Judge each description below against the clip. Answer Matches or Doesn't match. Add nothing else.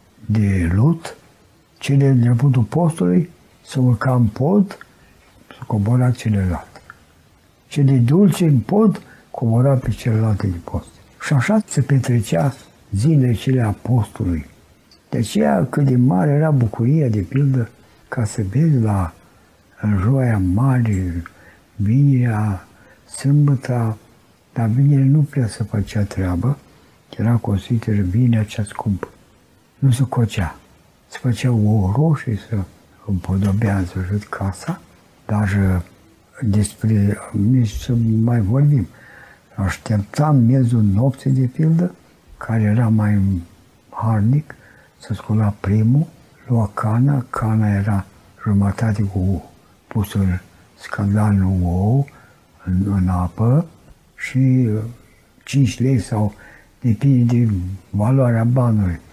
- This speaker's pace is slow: Matches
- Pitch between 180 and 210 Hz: Doesn't match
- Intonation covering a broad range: Doesn't match